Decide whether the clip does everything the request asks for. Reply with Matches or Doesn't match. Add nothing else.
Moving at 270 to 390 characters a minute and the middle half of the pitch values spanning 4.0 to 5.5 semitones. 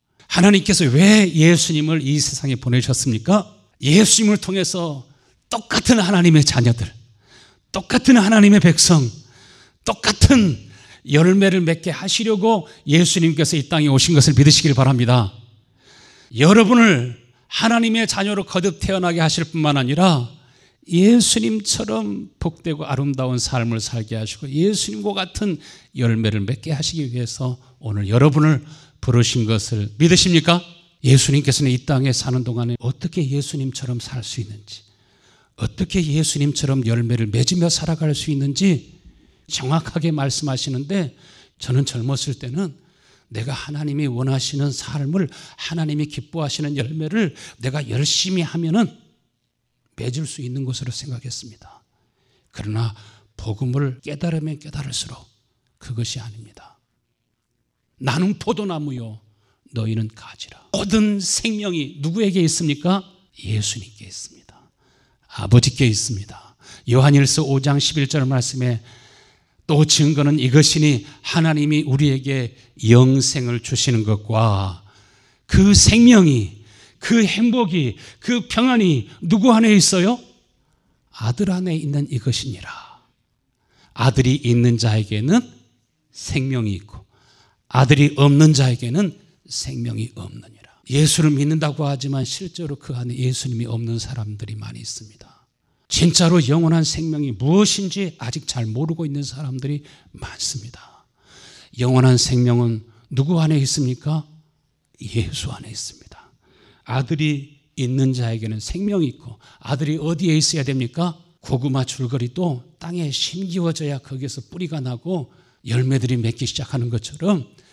Matches